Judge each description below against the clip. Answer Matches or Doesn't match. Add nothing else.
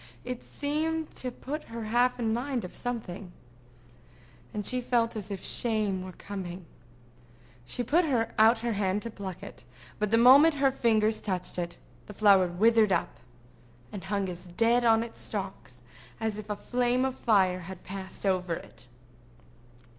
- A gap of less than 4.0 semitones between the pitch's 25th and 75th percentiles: Doesn't match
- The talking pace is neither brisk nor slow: Matches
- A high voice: Matches